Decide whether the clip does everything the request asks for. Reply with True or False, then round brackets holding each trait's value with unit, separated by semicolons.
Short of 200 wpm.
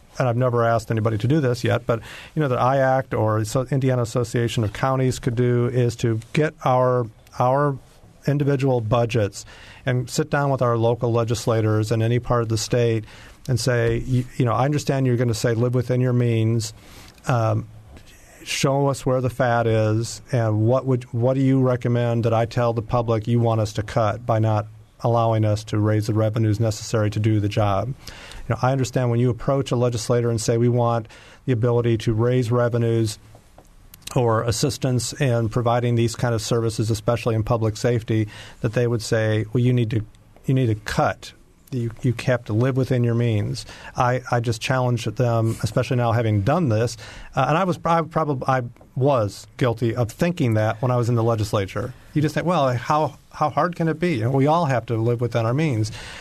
False (205 wpm)